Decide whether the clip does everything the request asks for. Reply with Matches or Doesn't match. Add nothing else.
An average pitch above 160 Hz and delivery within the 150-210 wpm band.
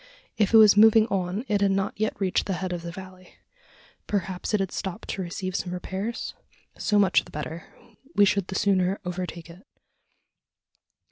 Matches